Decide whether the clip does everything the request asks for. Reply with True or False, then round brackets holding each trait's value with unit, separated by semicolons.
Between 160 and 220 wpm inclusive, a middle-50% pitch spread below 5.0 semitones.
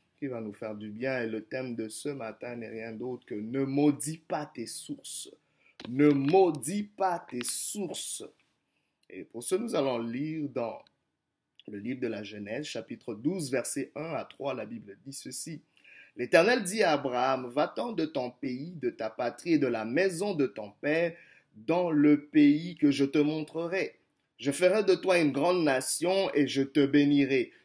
False (180 wpm; 5.3 semitones)